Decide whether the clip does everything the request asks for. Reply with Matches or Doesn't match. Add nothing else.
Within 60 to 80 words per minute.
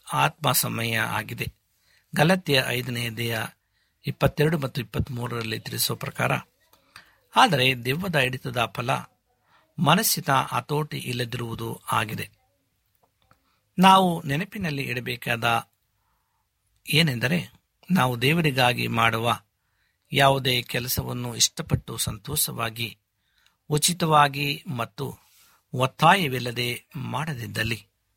Matches